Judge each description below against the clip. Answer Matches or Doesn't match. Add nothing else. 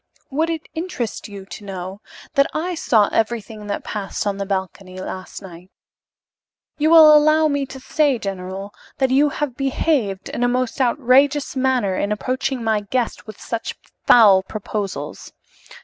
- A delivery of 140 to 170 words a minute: Matches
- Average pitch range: Doesn't match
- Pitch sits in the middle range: Doesn't match